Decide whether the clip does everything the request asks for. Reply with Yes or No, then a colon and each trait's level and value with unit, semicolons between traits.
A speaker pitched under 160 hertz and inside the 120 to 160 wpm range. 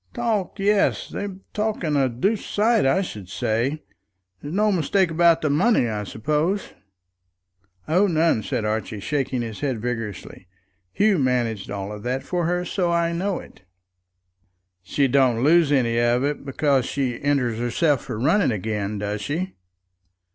Yes: medium, 140 Hz; average, 150 wpm